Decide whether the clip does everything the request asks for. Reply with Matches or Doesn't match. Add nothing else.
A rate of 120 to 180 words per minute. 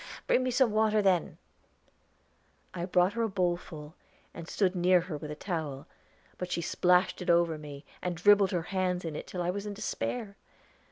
Doesn't match